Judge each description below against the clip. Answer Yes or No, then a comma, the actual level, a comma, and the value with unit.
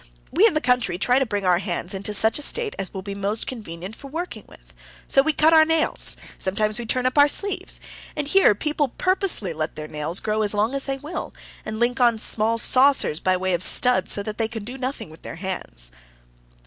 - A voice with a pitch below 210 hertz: No, high, 225 Hz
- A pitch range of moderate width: No, wide, 6.2 semitones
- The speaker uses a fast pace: Yes, fast, 225 wpm